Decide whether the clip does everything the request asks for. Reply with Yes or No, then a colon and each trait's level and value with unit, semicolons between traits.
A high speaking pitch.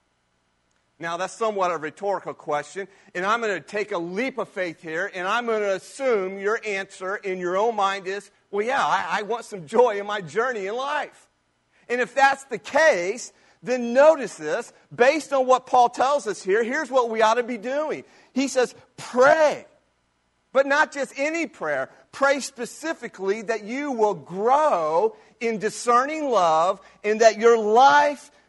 Yes: high, 225 Hz